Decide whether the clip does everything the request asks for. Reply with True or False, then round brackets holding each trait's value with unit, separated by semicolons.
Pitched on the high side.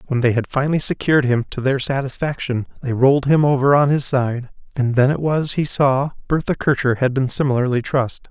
False (135 Hz)